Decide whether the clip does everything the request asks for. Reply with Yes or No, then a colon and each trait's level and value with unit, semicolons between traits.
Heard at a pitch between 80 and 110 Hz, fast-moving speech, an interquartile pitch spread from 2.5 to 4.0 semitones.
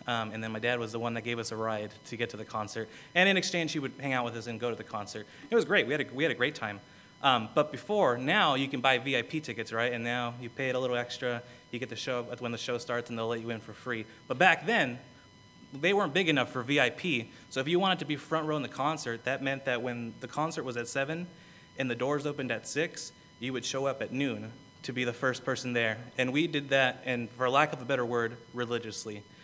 No: low, 125 Hz; fast, 275 wpm; average, 3.0 semitones